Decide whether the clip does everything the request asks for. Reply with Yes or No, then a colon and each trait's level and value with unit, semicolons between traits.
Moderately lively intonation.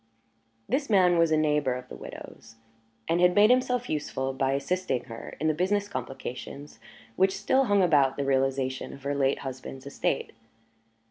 No: wide, 5.7 semitones